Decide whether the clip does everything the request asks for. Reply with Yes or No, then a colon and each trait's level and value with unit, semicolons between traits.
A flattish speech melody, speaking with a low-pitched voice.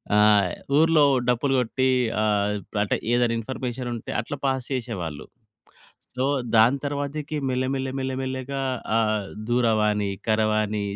No: average, 3.6 semitones; low, 125 Hz